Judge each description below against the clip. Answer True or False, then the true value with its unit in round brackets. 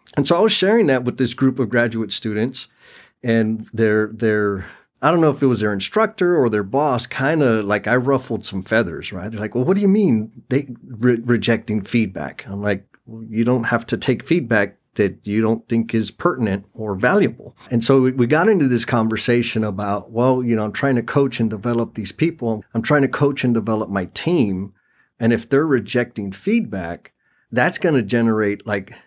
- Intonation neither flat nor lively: True (3.3 semitones)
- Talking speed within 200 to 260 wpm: True (205 wpm)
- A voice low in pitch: True (115 Hz)